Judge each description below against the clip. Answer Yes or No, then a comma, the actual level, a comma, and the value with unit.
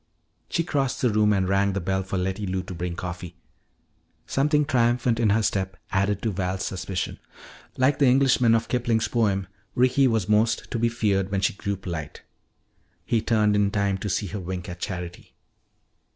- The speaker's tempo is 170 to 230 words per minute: Yes, average, 180 wpm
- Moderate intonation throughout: Yes, average, 3.7 semitones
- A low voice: Yes, low, 100 Hz